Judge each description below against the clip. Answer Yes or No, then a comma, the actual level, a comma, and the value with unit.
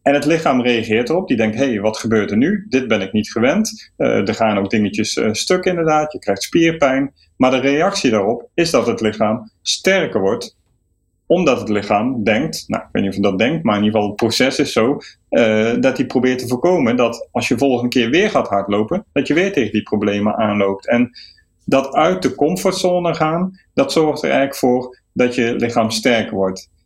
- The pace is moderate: No, fast, 215 wpm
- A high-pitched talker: No, low, 120 Hz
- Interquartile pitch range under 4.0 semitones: No, average, 5.2 semitones